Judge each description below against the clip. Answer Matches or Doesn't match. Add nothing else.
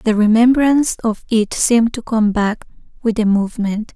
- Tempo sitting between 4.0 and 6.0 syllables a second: Matches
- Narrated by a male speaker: Doesn't match